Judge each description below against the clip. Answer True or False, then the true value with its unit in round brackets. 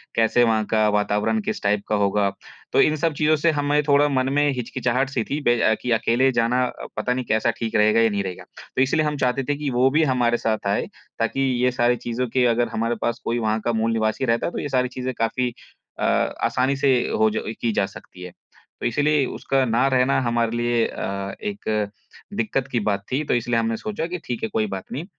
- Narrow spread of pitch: False (3.4 semitones)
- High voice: False (120 Hz)